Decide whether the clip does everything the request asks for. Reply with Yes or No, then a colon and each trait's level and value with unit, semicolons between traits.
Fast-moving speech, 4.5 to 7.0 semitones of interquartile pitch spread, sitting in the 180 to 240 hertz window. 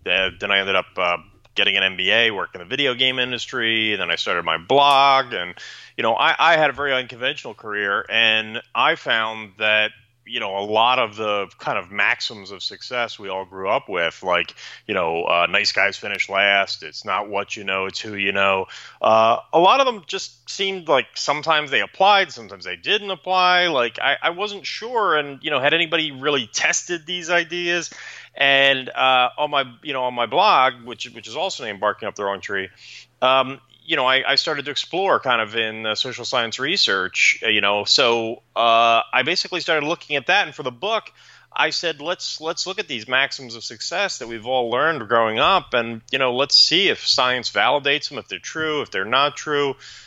No: fast, 210 wpm; wide, 5.4 semitones; low, 125 Hz